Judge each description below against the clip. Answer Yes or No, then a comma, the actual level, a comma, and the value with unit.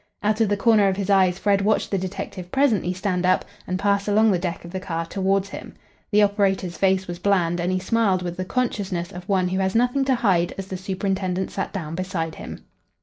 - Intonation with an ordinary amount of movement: No, narrow, 2.0 semitones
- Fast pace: Yes, fast, 225 wpm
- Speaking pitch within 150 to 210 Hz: Yes, high, 190 Hz